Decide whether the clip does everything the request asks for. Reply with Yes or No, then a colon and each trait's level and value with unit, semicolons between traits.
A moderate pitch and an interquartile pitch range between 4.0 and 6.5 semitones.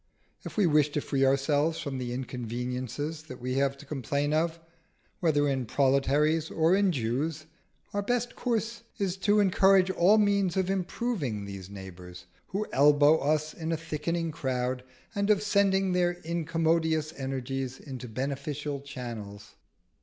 Yes: medium, 150 Hz; average, 4.9 semitones